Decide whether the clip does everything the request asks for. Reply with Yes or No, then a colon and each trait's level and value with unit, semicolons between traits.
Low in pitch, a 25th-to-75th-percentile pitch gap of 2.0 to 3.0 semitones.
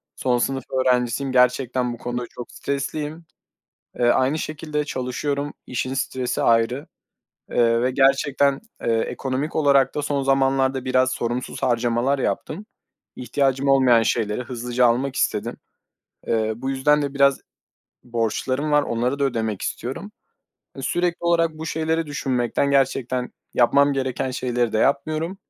Yes: low, 130 Hz; narrow, 2.4 semitones